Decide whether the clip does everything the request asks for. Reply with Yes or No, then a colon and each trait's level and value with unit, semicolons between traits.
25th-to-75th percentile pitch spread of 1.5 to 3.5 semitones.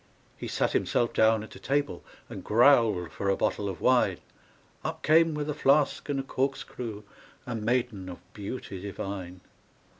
No: wide, 5.5 semitones